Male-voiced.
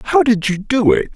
Yes: male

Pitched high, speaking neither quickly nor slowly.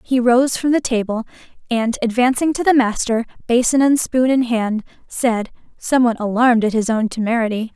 Yes: high, 240 Hz; average, 170 wpm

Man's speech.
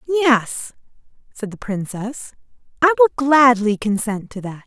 No: female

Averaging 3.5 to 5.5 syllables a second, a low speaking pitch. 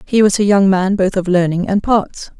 No: 4.9 syllables/s; high, 195 Hz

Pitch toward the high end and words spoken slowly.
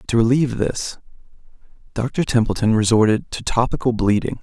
No: low, 115 Hz; slow, 120 wpm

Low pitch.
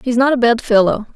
No: high, 235 Hz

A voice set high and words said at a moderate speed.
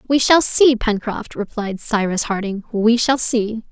Yes: high, 225 Hz; average, 160 wpm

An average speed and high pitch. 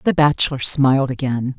No: average, 150 wpm; low, 130 Hz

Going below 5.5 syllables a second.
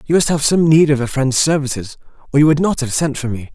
No: 6.2 syllables/s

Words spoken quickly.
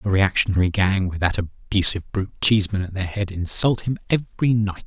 No: average, 185 wpm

